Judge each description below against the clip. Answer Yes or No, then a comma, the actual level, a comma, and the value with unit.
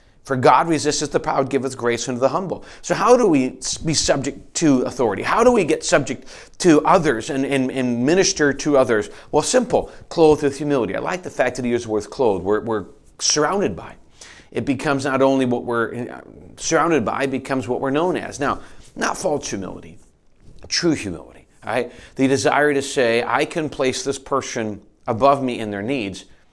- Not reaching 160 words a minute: No, average, 190 wpm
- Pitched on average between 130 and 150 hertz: Yes, low, 135 Hz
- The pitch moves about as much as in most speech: Yes, average, 3.5 semitones